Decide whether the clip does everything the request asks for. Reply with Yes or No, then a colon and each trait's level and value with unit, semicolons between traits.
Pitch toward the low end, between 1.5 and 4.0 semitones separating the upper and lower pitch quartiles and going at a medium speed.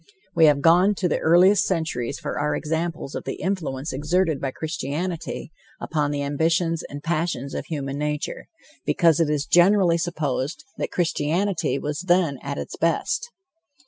No: medium, 160 Hz; average, 3.1 semitones; average, 155 wpm